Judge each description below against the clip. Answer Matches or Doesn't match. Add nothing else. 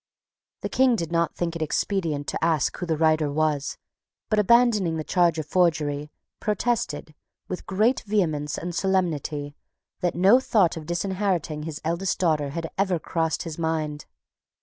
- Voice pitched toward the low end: Doesn't match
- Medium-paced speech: Matches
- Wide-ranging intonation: Doesn't match